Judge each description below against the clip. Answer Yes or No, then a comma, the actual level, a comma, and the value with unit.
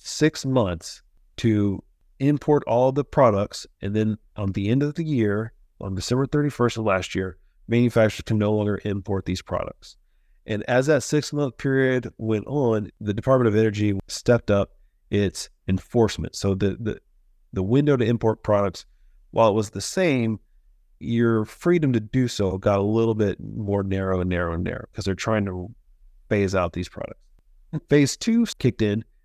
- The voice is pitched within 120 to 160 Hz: No, low, 110 Hz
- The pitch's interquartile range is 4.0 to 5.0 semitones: Yes, average, 4.4 semitones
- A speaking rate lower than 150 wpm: No, average, 170 wpm